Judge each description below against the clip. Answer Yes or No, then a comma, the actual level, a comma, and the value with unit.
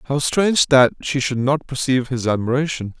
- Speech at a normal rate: Yes, average, 180 wpm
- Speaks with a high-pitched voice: No, low, 135 Hz